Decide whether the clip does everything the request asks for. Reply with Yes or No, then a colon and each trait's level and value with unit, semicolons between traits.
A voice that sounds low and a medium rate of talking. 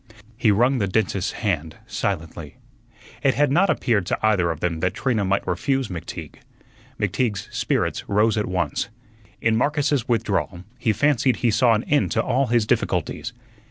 Yes: low, 110 Hz; average, 160 wpm